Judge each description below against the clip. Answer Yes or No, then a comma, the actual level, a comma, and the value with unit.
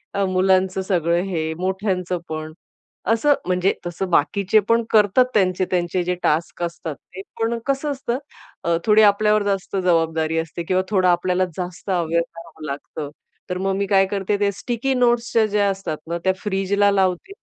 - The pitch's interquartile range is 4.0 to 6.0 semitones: No, average, 2.9 semitones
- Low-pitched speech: No, high, 190 Hz